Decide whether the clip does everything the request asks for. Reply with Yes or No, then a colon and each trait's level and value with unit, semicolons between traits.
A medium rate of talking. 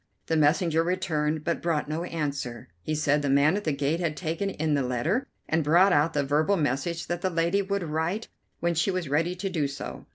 No: fast, 220 wpm